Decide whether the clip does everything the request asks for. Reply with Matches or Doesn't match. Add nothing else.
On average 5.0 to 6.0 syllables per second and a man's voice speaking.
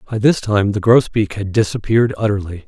Matches